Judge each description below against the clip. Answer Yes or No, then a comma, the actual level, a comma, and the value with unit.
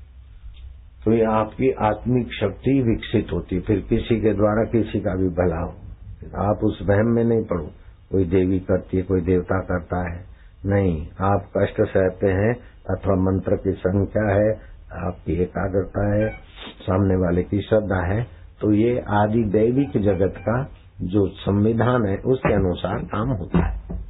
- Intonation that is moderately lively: Yes, average, 3.0 semitones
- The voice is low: Yes, very low, 95 Hz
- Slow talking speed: No, average, 160 wpm